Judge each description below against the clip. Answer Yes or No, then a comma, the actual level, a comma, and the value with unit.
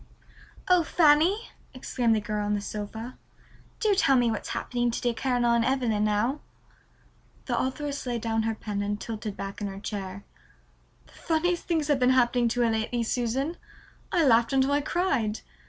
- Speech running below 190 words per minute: Yes, average, 170 wpm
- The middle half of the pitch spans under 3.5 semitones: No, average, 4.4 semitones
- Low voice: No, high, 240 Hz